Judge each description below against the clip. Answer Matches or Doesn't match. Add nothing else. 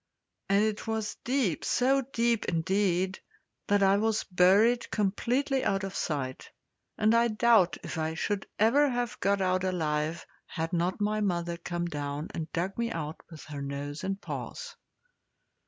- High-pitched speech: Matches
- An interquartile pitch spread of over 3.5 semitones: Matches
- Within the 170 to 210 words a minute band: Doesn't match